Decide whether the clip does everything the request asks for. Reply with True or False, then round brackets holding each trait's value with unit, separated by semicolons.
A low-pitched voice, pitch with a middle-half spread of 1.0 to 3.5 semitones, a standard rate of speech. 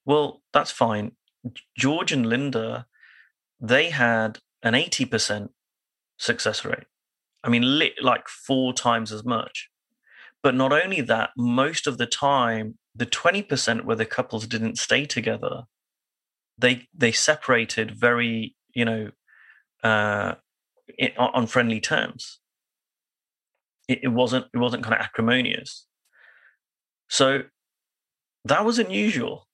False (120 Hz; 3.1 semitones; 115 wpm)